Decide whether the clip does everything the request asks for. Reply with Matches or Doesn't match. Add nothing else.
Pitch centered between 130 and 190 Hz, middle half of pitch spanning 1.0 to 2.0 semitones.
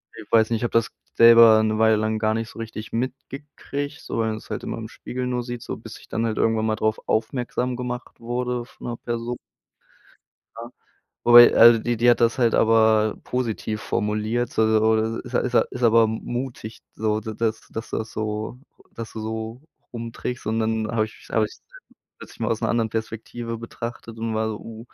Doesn't match